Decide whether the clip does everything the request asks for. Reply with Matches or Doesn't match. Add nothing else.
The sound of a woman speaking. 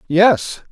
Doesn't match